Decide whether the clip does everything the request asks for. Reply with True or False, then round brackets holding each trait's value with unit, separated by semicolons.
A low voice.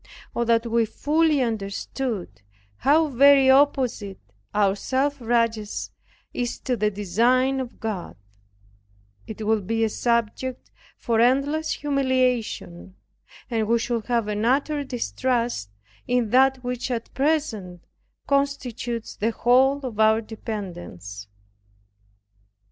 False (235 Hz)